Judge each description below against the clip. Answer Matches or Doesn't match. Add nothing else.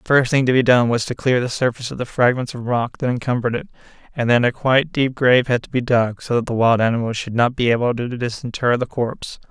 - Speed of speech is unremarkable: Doesn't match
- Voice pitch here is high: Doesn't match